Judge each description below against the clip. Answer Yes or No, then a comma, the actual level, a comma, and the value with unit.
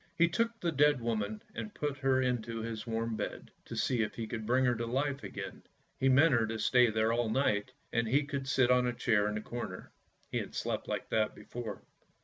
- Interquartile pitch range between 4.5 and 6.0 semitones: No, average, 3.3 semitones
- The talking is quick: Yes, fast, 225 wpm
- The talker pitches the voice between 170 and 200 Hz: No, low, 120 Hz